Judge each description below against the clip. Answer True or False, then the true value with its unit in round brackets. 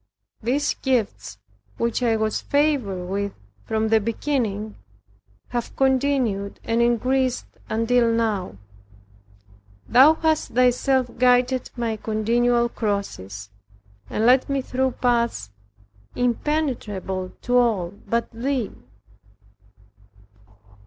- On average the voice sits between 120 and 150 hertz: False (235 Hz)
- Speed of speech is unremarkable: False (95 wpm)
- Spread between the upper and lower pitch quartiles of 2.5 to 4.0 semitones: True (3.1 semitones)